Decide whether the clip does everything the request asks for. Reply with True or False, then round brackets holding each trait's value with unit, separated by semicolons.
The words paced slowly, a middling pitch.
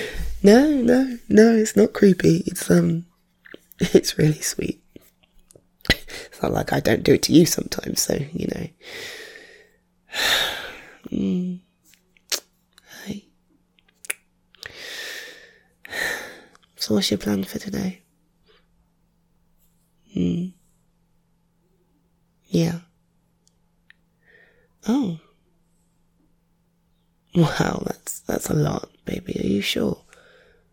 True (85 wpm; 175 Hz)